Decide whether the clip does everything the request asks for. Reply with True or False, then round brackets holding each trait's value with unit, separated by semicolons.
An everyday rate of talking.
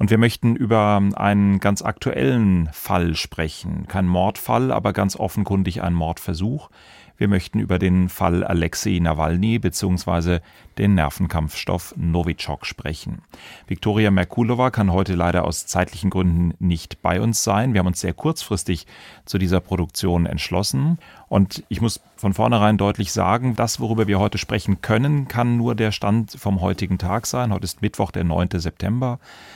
True (155 wpm)